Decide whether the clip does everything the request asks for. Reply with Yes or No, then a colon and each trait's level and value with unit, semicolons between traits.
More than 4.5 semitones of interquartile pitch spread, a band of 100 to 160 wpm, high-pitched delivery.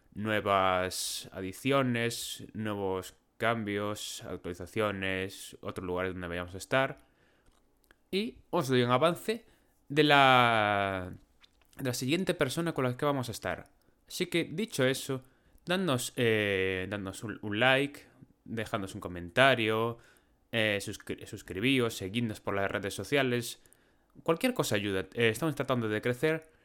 No: wide, 5.5 semitones; slow, 125 wpm; low, 115 Hz